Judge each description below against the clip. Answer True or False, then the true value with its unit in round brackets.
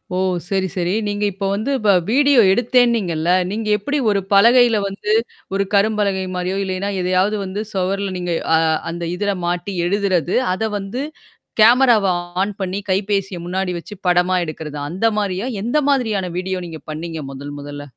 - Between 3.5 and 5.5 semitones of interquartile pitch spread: False (2.8 semitones)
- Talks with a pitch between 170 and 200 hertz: True (195 Hz)